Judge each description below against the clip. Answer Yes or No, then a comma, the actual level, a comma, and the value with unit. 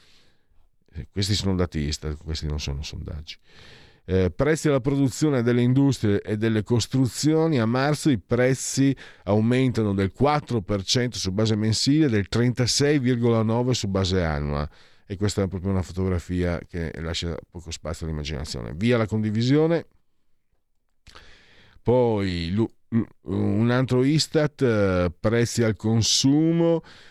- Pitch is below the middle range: Yes, low, 110 Hz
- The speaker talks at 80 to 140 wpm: Yes, average, 120 wpm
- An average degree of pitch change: No, wide, 5.7 semitones